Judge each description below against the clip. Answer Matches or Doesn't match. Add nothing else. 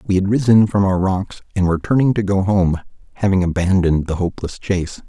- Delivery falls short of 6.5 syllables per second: Matches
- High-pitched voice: Doesn't match